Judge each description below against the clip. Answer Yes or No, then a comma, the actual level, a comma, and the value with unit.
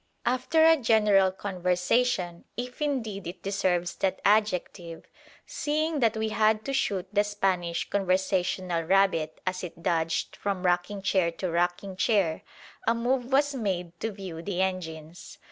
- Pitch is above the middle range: Yes, high, 195 Hz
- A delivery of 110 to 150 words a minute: Yes, average, 145 wpm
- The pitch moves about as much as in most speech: Yes, average, 3.7 semitones